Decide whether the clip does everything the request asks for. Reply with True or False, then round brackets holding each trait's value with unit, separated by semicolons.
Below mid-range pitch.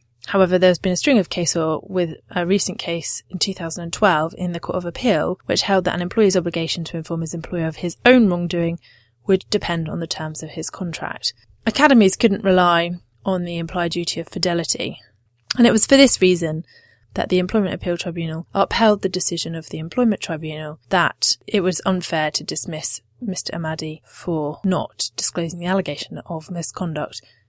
False (175 Hz)